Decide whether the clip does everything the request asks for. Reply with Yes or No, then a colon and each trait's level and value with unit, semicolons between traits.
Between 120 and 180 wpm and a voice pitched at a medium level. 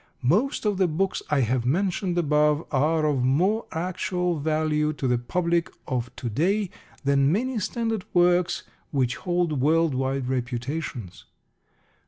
Yes: average, 140 wpm; medium, 155 Hz